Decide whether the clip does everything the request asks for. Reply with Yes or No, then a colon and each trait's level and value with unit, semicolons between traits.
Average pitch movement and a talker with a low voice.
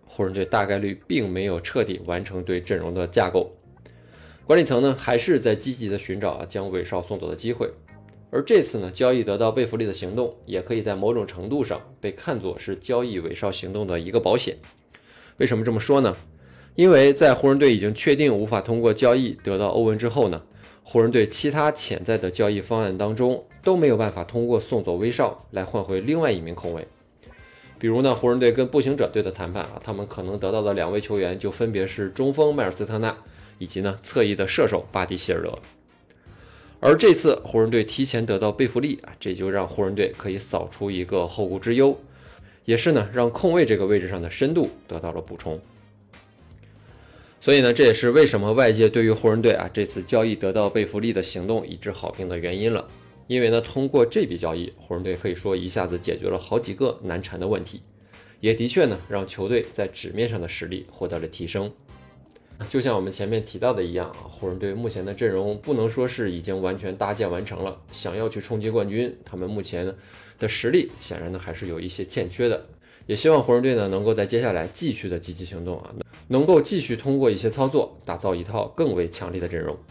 Yes: average, 4.1 semitones; low, 105 Hz